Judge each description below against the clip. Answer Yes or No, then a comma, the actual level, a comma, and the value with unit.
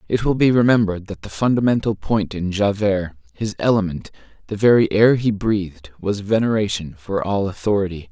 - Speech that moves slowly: No, average, 165 wpm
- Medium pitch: No, low, 100 Hz